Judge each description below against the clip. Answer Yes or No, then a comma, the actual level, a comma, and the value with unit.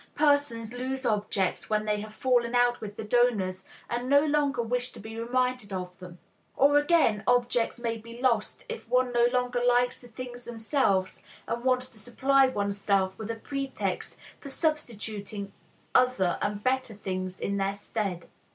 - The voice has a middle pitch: No, high, 235 Hz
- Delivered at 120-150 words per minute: No, average, 165 wpm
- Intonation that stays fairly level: No, average, 3.6 semitones